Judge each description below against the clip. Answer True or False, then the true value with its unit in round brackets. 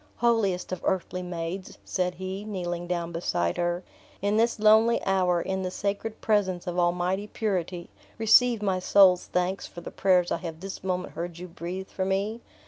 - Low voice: False (185 Hz)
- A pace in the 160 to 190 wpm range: True (175 wpm)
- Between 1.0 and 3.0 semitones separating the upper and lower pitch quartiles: True (2.4 semitones)